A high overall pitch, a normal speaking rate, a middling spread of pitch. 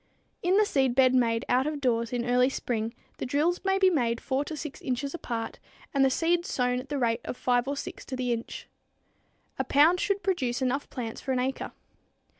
No: very high, 260 Hz; fast, 210 wpm; average, 3.3 semitones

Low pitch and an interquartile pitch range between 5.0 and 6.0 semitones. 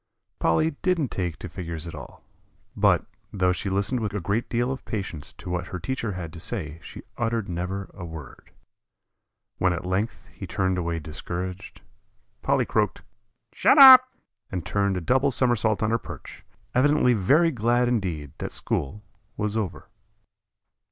Yes: low, 100 Hz; average, 5.3 semitones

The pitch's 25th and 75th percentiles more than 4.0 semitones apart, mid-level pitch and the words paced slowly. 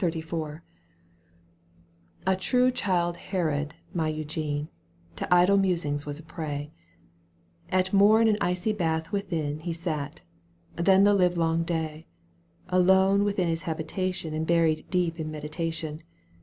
No: average, 3.0 semitones; medium, 165 Hz; slow, 130 wpm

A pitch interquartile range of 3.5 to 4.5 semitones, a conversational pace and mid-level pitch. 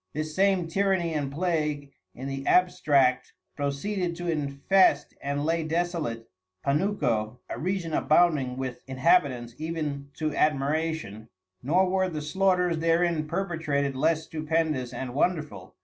No: average, 3.8 semitones; slow, 125 wpm; medium, 155 Hz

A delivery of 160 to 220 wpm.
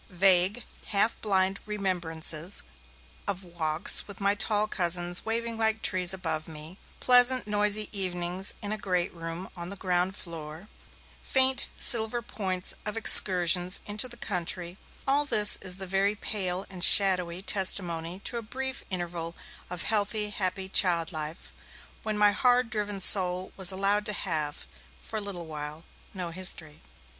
No: average, 150 wpm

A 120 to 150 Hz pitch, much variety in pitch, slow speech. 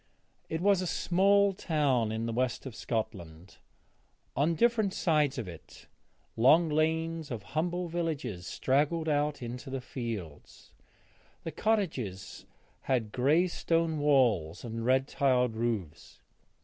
Yes: low, 135 Hz; wide, 6.2 semitones; slow, 125 wpm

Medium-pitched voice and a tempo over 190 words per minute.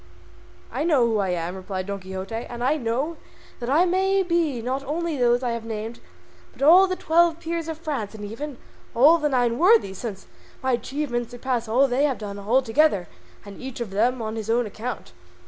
No: high, 245 Hz; fast, 205 wpm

